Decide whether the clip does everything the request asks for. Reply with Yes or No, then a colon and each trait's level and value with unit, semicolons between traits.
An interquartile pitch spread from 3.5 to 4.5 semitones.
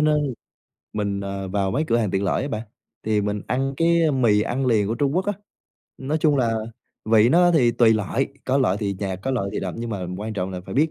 No: average, 5.2 semitones